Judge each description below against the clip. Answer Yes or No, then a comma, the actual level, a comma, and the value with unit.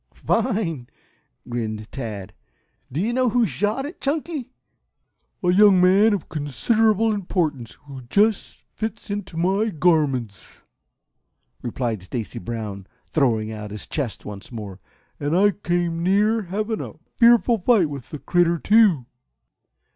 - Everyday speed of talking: No, slow, 130 wpm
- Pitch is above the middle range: No, medium, 175 Hz